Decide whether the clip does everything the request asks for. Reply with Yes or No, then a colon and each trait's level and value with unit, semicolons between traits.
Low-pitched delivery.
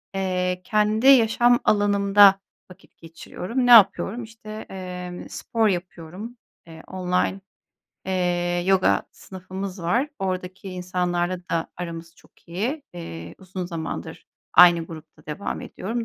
No: medium, 185 Hz